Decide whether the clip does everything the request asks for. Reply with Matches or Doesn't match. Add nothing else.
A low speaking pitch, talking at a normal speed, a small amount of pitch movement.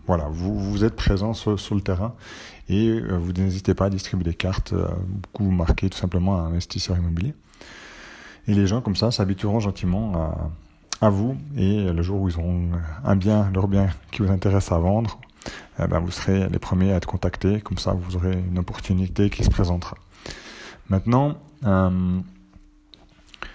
Matches